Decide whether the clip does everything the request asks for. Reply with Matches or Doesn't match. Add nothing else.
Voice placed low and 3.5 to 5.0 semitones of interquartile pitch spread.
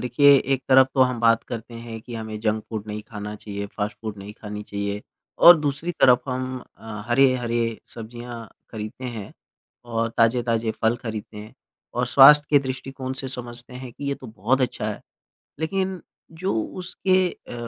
Doesn't match